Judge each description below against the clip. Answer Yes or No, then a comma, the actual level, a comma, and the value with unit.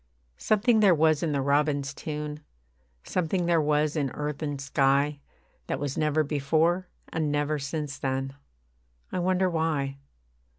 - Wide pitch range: No, narrow, 2.5 semitones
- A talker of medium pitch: Yes, medium, 150 Hz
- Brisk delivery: No, average, 140 wpm